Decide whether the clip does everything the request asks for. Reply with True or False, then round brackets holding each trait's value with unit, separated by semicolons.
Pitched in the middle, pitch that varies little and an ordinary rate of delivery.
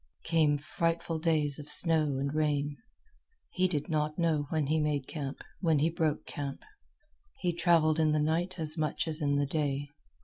True (155 Hz; 2.0 semitones; 175 wpm)